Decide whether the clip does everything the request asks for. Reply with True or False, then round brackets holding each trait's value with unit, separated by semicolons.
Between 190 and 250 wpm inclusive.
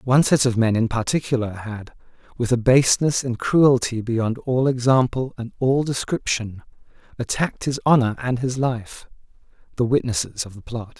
False (160 wpm)